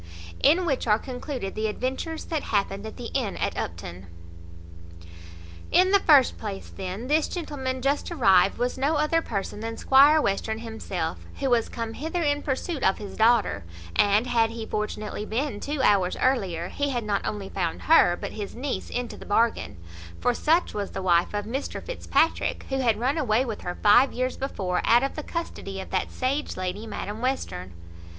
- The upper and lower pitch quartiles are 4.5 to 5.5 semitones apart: Yes, average, 5.2 semitones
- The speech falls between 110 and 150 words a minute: No, average, 185 wpm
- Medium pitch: No, high, 235 Hz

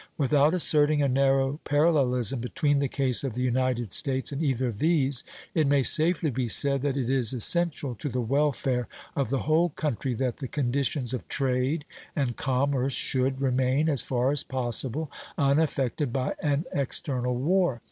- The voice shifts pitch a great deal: No, narrow, 2.5 semitones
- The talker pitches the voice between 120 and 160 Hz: Yes, low, 135 Hz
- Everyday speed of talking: Yes, average, 165 wpm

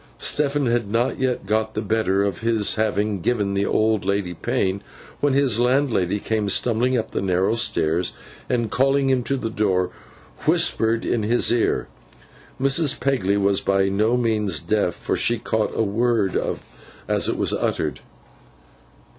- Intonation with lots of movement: No, average, 3.5 semitones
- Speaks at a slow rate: No, average, 155 wpm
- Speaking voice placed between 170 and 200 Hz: No, low, 110 Hz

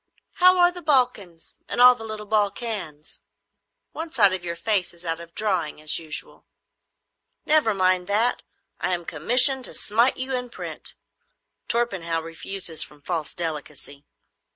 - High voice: Yes, high, 195 Hz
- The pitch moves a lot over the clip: Yes, wide, 6.6 semitones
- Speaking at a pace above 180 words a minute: No, average, 150 wpm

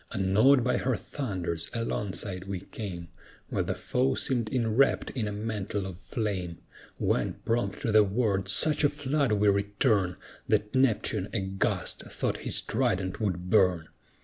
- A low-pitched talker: Yes, low, 105 Hz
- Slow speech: No, average, 150 wpm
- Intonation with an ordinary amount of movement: Yes, average, 3.9 semitones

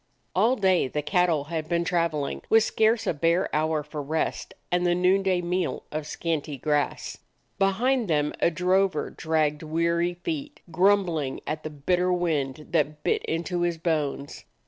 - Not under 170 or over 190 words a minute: No, average, 155 wpm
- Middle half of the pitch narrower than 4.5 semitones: Yes, average, 3.1 semitones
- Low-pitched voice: No, medium, 170 Hz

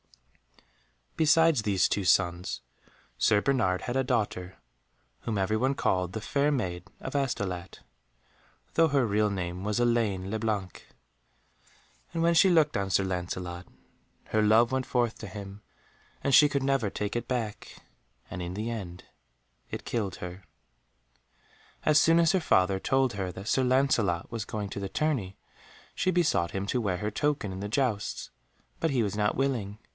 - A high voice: No, low, 110 Hz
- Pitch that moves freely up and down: Yes, wide, 5.7 semitones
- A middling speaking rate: Yes, average, 165 wpm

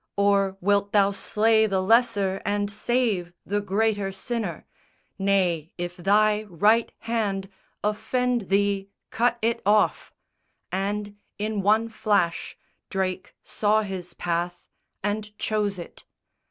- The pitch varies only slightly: Yes, narrow, 1.9 semitones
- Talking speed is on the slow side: Yes, slow, 115 wpm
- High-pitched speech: Yes, high, 205 Hz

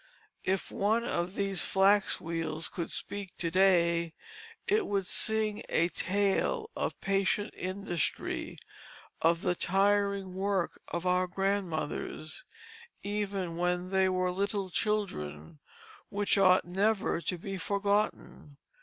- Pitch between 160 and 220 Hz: Yes, high, 190 Hz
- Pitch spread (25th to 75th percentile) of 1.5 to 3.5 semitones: Yes, narrow, 2.6 semitones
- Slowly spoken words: Yes, slow, 120 wpm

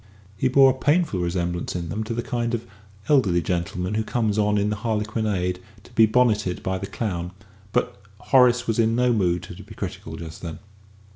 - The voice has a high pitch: No, low, 105 Hz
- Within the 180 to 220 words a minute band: Yes, average, 195 wpm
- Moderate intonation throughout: Yes, average, 4.8 semitones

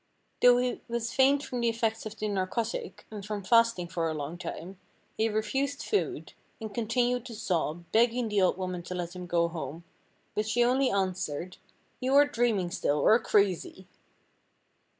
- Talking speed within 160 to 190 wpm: Yes, average, 170 wpm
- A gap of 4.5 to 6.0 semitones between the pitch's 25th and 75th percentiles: Yes, average, 4.9 semitones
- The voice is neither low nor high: No, high, 215 Hz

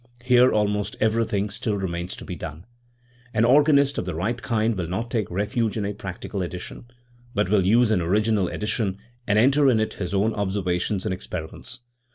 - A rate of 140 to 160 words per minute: No, average, 185 wpm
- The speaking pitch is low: Yes, low, 105 Hz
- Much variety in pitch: No, average, 3.5 semitones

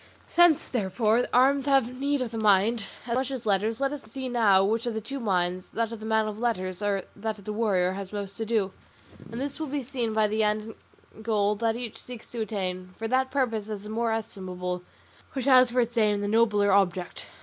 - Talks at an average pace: No, fast, 225 wpm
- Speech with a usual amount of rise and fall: Yes, average, 3.2 semitones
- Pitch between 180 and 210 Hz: No, high, 220 Hz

